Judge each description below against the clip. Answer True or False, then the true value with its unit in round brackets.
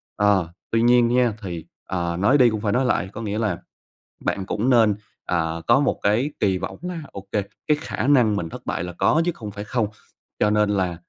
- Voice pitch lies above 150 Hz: False (105 Hz)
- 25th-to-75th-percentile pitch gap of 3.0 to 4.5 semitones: True (4.2 semitones)